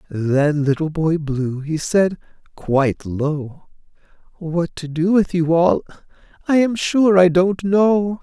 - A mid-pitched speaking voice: Yes, medium, 165 Hz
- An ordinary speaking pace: Yes, average, 145 wpm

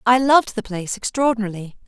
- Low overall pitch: No, high, 225 Hz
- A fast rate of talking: No, average, 160 wpm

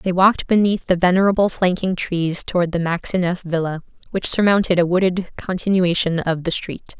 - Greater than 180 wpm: No, average, 165 wpm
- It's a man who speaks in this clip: No, female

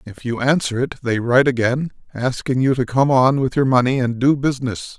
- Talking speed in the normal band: No, fast, 215 wpm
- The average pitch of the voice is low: Yes, low, 130 Hz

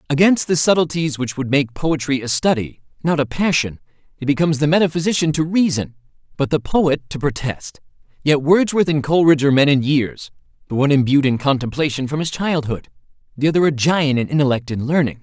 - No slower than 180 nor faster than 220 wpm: Yes, average, 185 wpm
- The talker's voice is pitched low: No, medium, 145 Hz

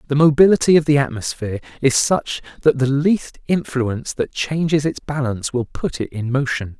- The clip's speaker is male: Yes, male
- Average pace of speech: Yes, average, 175 wpm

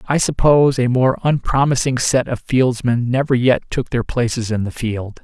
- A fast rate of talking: No, average, 185 wpm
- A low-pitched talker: Yes, low, 125 Hz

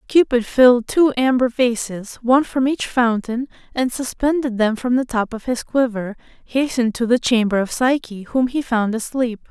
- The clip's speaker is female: Yes, female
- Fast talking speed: No, average, 175 wpm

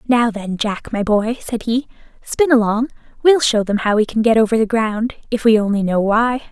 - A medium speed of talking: No, fast, 220 wpm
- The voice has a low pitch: No, high, 225 Hz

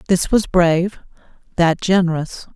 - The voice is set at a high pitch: No, medium, 175 Hz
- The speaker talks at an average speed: No, slow, 115 wpm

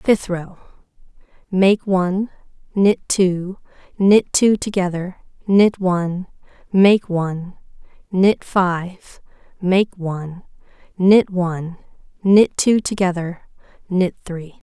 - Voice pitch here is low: No, medium, 185 Hz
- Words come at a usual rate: No, slow, 95 wpm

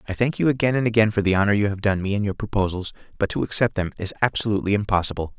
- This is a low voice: Yes, low, 105 Hz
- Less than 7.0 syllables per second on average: No, 7.4 syllables/s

